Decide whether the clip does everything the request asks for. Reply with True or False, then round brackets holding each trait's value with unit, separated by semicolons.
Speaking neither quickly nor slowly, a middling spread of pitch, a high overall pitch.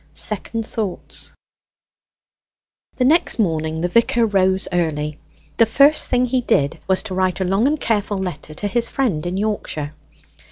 True (155 wpm; 4.9 semitones; 195 Hz)